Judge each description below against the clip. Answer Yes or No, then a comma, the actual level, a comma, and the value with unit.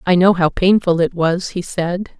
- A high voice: No, medium, 180 Hz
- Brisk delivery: Yes, fast, 220 wpm